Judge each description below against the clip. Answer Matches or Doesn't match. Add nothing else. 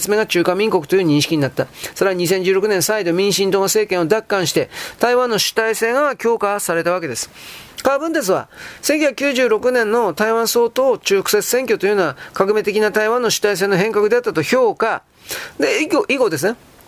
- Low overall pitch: Doesn't match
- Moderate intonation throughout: Doesn't match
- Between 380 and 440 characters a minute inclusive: Doesn't match